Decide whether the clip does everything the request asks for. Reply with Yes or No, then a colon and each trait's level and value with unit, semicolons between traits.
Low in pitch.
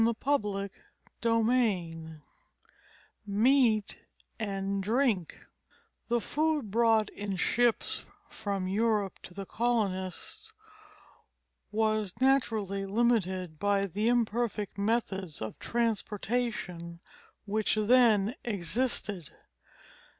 No: high, 215 Hz